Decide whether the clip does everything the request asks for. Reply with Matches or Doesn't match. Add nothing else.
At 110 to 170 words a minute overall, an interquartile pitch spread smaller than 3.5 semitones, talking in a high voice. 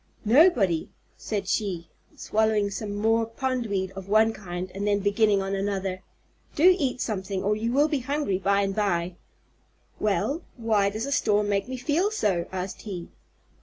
Matches